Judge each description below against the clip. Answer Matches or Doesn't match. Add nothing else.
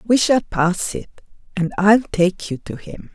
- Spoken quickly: Doesn't match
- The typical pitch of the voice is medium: Doesn't match